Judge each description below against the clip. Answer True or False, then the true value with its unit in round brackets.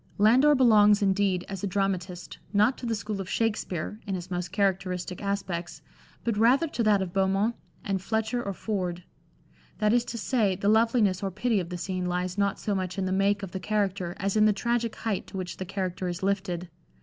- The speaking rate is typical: False (210 wpm)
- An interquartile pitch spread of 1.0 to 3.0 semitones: True (2.5 semitones)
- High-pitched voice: True (195 Hz)